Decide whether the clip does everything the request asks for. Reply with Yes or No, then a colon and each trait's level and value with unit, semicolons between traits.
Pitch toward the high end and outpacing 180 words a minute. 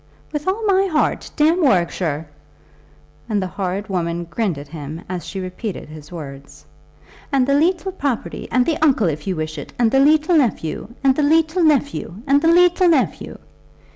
No: high, 245 Hz; average, 175 wpm